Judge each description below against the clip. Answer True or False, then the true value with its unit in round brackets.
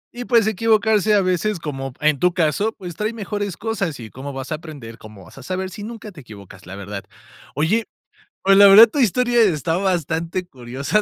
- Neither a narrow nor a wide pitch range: False (7.5 semitones)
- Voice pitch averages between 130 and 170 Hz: False (180 Hz)